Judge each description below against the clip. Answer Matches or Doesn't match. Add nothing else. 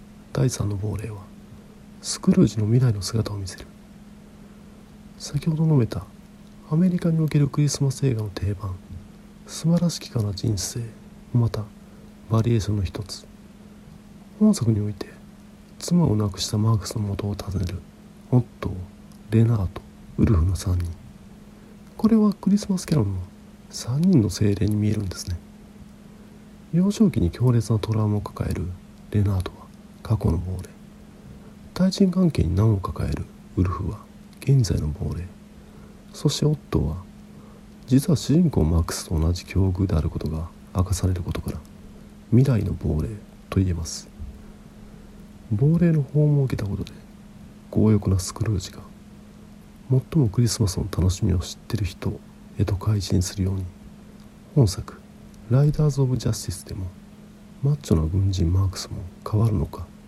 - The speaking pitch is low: Matches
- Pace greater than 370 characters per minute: Doesn't match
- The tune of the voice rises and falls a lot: Matches